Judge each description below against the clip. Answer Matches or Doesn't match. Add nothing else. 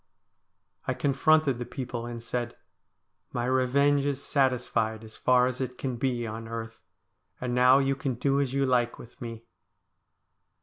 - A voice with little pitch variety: Matches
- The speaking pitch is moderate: Doesn't match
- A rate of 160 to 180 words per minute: Matches